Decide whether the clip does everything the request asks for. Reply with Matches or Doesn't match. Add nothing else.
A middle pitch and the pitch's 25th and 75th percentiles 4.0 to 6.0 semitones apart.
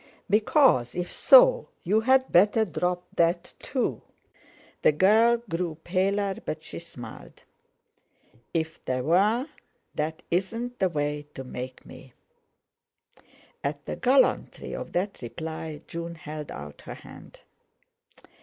Matches